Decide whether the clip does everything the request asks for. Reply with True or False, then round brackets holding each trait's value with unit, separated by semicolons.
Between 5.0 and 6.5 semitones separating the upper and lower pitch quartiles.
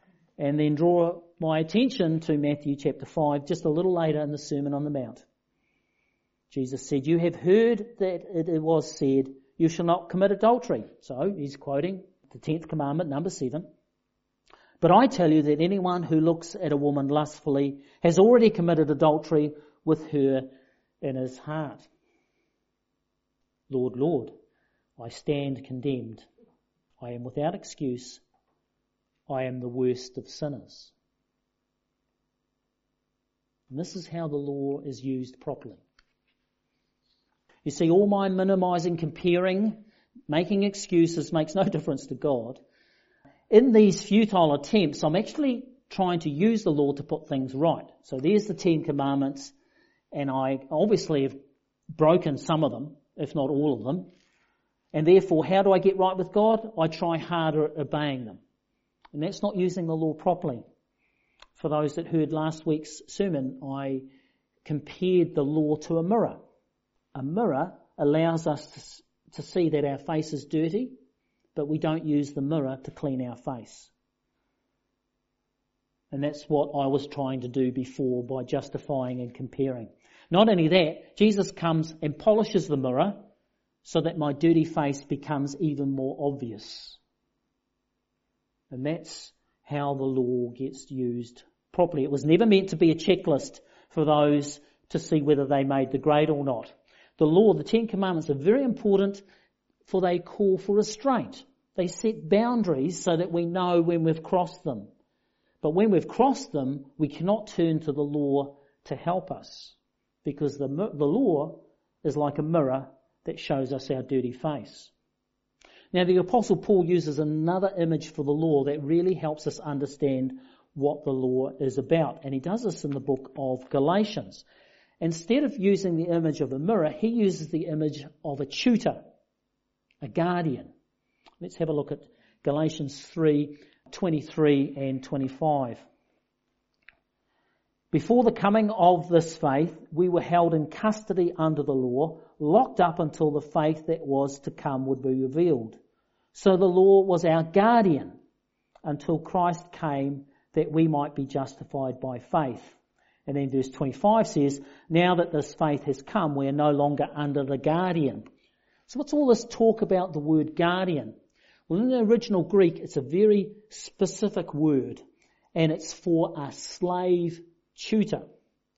False (4.2 semitones)